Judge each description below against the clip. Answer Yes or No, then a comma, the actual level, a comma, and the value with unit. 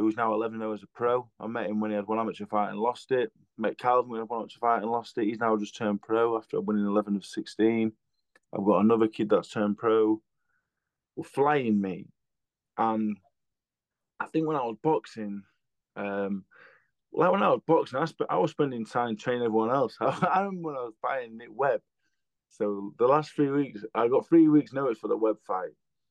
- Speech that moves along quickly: Yes, fast, 215 wpm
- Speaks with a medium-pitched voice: No, low, 115 Hz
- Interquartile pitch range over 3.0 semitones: No, average, 2.7 semitones